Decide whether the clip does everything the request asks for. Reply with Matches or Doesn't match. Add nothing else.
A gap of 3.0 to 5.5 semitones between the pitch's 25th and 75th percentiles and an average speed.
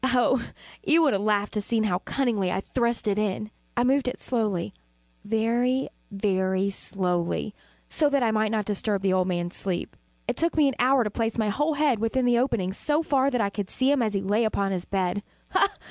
Doesn't match